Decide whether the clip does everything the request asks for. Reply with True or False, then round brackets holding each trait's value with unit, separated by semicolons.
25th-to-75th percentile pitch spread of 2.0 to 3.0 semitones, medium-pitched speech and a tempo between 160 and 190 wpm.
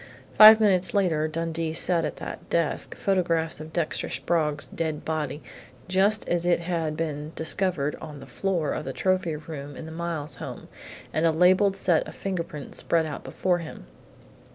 True (2.7 semitones; 165 Hz; 170 wpm)